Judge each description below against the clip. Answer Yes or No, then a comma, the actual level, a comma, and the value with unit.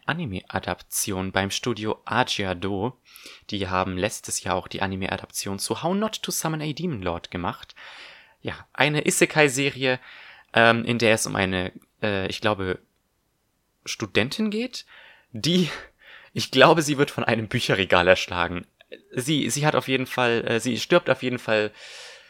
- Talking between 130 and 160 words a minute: Yes, average, 150 wpm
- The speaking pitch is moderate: No, low, 115 Hz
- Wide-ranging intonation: Yes, wide, 6.7 semitones